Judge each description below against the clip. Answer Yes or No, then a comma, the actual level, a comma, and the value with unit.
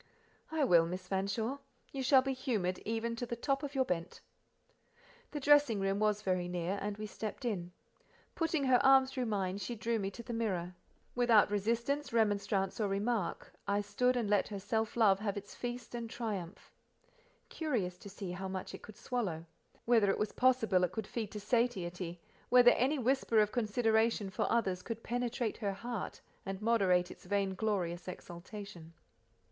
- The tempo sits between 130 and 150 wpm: No, average, 170 wpm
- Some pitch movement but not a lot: Yes, average, 4.0 semitones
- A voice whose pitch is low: No, high, 215 Hz